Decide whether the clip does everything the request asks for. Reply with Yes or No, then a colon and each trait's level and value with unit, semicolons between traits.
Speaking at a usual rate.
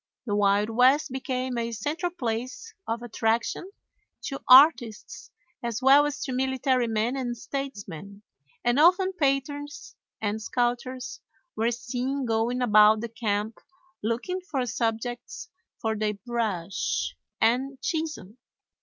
No: slow, 120 wpm